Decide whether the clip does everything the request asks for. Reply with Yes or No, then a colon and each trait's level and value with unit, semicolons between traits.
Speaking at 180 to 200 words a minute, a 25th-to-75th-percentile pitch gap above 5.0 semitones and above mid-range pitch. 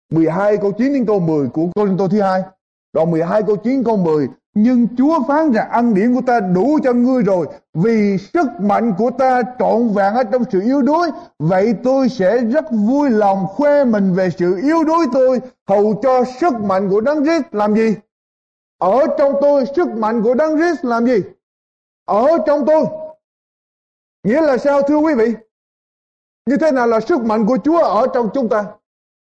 Yes: average, 195 wpm; wide, 5.5 semitones; high, 235 Hz